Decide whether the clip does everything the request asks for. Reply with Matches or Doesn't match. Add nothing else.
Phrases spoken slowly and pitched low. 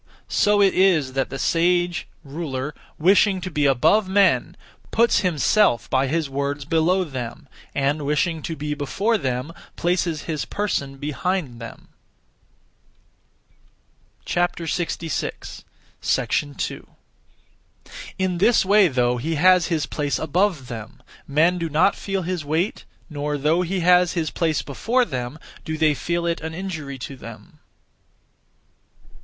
Doesn't match